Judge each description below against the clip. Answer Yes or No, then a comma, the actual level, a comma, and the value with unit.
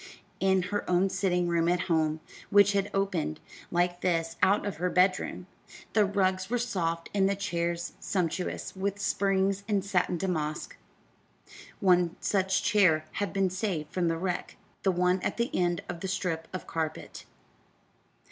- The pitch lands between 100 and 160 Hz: No, medium, 185 Hz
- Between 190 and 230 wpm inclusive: No, average, 155 wpm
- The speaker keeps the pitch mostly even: Yes, narrow, 2.3 semitones